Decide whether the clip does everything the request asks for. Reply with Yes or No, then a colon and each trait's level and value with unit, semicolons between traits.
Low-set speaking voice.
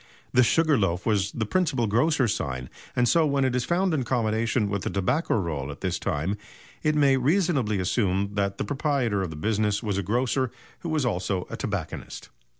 Yes: low, 115 Hz